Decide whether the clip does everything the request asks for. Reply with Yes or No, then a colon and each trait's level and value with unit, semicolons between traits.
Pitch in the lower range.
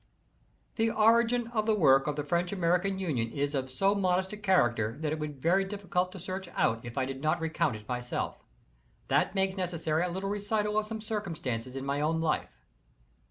No: medium, 175 Hz